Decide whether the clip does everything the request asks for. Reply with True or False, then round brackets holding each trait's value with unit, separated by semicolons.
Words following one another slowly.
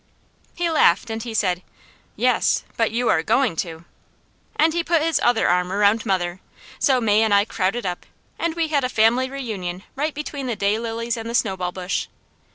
False (185 wpm)